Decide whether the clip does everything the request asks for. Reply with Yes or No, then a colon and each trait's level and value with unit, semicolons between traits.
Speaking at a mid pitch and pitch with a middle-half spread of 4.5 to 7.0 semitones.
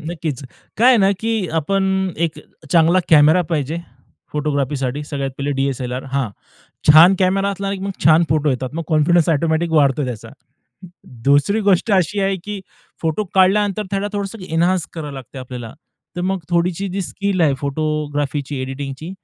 Yes: medium, 160 Hz; average, 5.1 semitones